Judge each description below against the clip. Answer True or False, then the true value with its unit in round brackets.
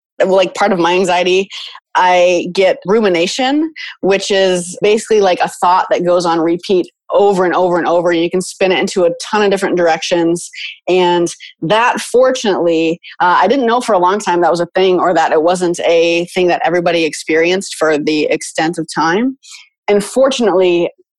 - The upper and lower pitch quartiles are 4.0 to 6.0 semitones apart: False (2.8 semitones)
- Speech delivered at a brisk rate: False (185 wpm)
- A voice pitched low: False (180 Hz)